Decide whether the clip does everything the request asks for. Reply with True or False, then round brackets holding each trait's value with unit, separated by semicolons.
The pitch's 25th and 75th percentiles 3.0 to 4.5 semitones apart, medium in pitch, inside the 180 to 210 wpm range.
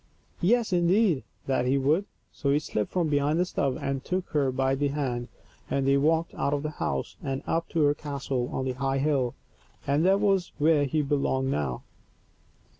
True (3.4 semitones; 145 Hz; 190 wpm)